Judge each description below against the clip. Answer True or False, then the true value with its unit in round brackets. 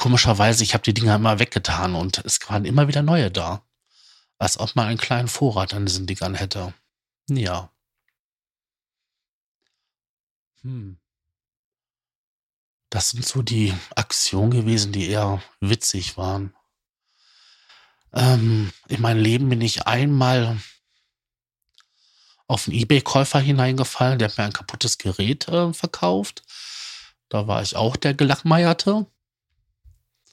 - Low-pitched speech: True (115 Hz)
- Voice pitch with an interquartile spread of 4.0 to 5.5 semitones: True (4.3 semitones)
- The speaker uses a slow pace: True (120 wpm)